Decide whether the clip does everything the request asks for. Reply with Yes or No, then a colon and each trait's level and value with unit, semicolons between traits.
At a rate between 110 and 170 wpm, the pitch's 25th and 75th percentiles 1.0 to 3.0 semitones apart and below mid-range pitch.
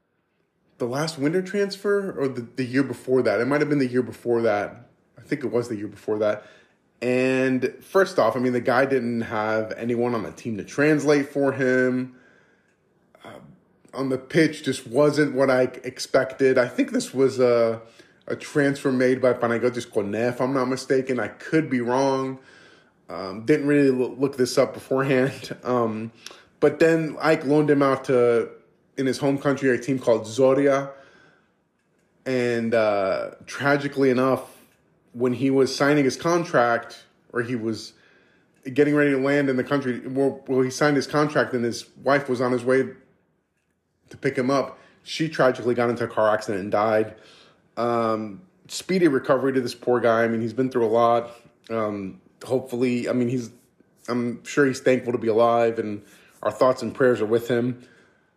No: average, 180 wpm; average, 2.7 semitones; low, 130 Hz